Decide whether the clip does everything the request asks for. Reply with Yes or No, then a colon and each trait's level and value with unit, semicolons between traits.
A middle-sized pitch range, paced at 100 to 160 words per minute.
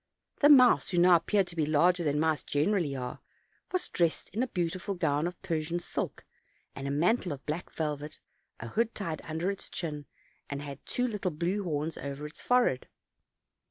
No: average, 4.3 semitones; average, 190 wpm